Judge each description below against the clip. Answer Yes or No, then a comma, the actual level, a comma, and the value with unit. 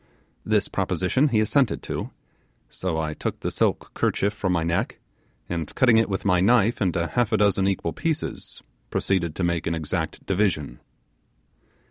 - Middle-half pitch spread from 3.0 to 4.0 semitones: No, average, 4.4 semitones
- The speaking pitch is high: No, very low, 95 Hz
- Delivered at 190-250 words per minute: No, average, 160 wpm